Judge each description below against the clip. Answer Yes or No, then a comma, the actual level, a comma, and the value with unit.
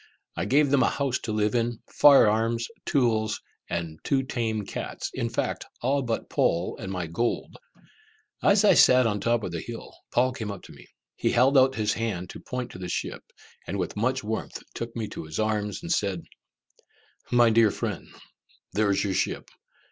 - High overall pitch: No, low, 115 Hz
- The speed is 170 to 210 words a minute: Yes, average, 200 wpm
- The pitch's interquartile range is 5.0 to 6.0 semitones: No, average, 3.8 semitones